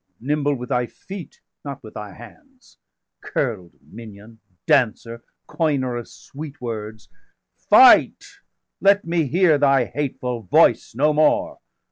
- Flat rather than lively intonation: No, average, 4.9 semitones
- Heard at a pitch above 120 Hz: Yes, low, 135 Hz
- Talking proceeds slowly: Yes, slow, 120 wpm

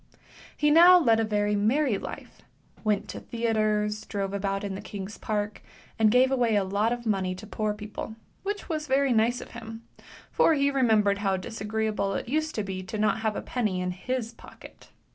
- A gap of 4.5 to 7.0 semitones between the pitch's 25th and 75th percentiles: No, average, 3.2 semitones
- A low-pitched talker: No, high, 215 Hz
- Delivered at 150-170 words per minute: No, average, 200 wpm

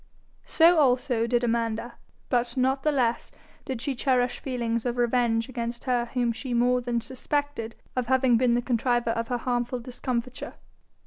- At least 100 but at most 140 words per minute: No, average, 165 wpm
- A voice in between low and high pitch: No, high, 245 Hz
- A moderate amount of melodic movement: No, narrow, 1.5 semitones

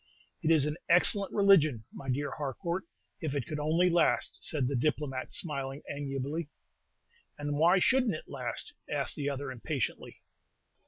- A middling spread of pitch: Yes, average, 3.4 semitones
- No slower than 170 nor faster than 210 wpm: No, average, 155 wpm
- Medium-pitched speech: Yes, medium, 150 Hz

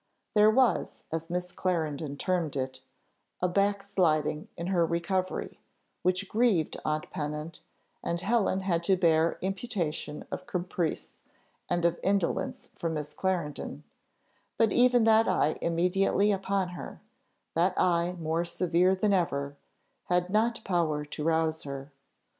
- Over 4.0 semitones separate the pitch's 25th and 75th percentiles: No, average, 3.3 semitones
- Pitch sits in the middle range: Yes, medium, 175 Hz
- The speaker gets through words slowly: Yes, slow, 130 wpm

